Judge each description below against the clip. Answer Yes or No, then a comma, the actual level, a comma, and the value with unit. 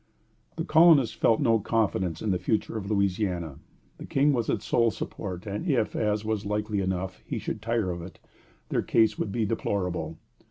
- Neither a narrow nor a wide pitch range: Yes, average, 3.5 semitones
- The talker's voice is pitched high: No, low, 105 Hz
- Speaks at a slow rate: No, average, 190 wpm